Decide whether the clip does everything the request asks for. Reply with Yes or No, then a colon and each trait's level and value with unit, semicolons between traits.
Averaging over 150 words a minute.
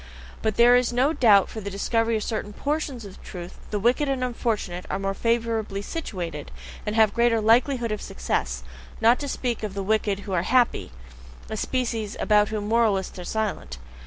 Yes: average, 190 wpm